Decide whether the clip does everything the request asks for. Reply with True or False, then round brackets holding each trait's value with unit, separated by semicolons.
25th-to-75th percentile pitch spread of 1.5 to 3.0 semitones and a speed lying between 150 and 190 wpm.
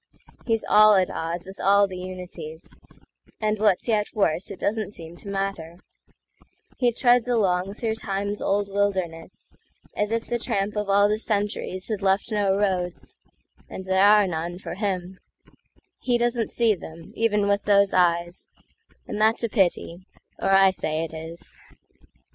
False (2.7 semitones; 140 wpm)